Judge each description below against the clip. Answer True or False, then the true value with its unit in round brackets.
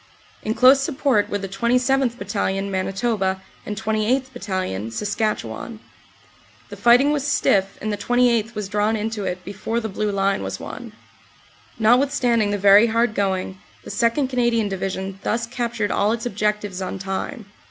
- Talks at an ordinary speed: True (155 wpm)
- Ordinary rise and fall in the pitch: True (3.4 semitones)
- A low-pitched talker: False (215 Hz)